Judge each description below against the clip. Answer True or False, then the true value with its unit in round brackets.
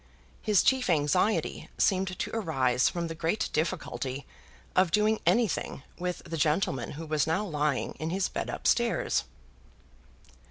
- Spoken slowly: False (145 wpm)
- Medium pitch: True (165 Hz)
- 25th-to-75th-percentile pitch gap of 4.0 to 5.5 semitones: True (4.4 semitones)